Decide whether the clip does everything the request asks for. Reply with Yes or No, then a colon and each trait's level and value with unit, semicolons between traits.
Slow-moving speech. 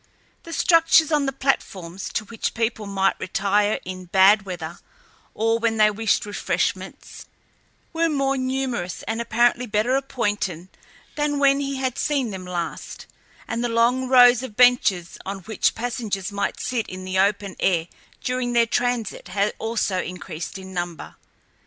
No: average, 150 wpm